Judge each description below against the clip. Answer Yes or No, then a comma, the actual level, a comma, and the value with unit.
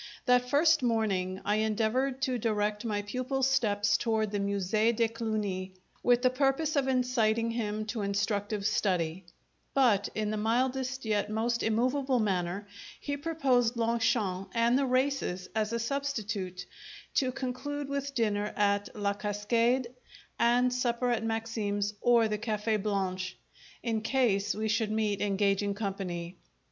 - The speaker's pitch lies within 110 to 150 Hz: No, high, 220 Hz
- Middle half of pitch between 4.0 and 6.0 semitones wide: No, average, 3.5 semitones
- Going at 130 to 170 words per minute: Yes, average, 140 wpm